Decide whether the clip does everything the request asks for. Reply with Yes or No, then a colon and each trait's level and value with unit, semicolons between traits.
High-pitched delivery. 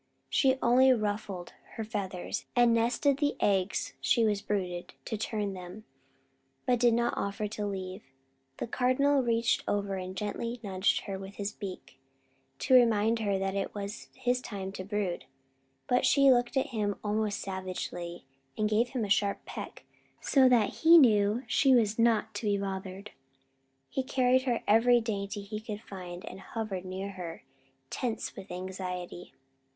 Yes: high, 210 Hz